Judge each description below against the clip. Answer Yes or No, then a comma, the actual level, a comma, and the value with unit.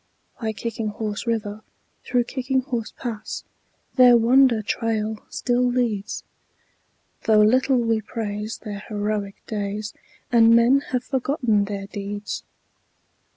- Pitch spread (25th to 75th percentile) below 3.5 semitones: Yes, average, 2.7 semitones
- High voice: Yes, high, 225 Hz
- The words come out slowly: Yes, slow, 115 wpm